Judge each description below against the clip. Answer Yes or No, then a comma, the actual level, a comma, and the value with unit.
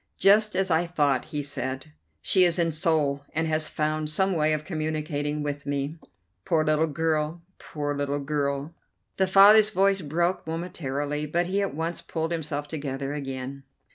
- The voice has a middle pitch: Yes, medium, 155 Hz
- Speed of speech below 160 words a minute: No, average, 165 wpm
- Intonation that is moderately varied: Yes, average, 3.0 semitones